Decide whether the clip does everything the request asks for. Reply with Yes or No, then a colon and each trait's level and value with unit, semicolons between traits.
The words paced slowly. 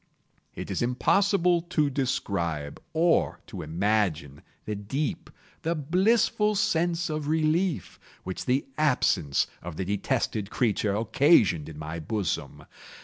Yes: slow, 120 wpm